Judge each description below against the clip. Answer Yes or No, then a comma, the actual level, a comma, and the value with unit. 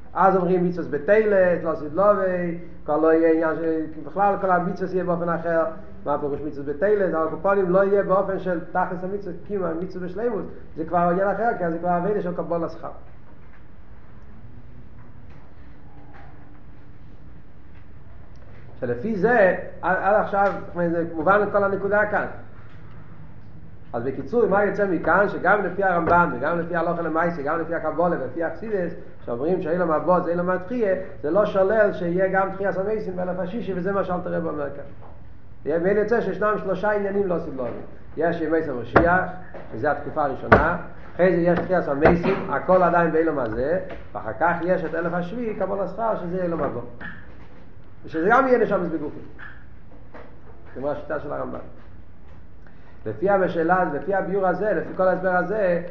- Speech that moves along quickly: Yes, fast, 155 wpm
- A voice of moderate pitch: Yes, medium, 175 Hz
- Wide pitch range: No, average, 3.4 semitones